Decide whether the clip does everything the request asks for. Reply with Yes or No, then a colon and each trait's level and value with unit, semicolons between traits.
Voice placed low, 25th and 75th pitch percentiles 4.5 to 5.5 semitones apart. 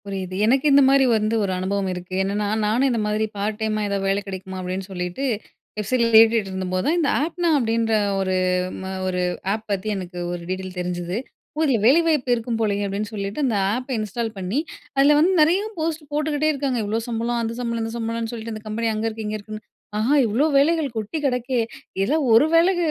No: high, 225 Hz; average, 5.2 semitones